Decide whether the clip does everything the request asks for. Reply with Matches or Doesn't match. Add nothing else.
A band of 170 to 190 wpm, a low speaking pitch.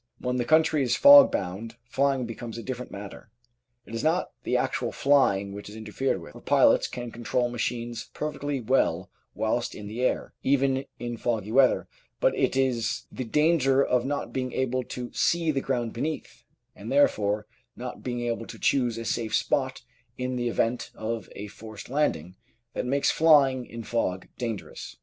Matches